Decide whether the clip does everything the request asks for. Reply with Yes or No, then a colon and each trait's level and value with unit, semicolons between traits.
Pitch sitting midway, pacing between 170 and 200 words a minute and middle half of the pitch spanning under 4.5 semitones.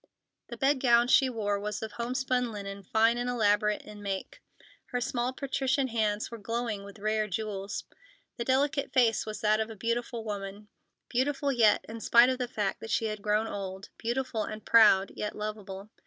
No: high, 220 Hz; average, 185 wpm; average, 2.9 semitones